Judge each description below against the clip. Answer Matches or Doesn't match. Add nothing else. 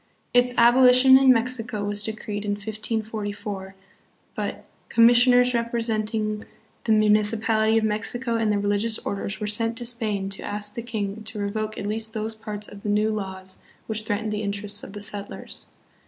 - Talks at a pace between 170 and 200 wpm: Matches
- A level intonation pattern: Matches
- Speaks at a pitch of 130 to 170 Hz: Doesn't match